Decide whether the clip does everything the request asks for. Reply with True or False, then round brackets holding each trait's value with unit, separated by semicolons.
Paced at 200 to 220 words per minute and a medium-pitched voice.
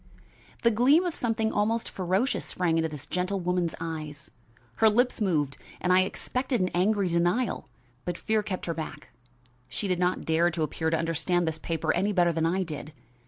False (185 wpm; 180 Hz)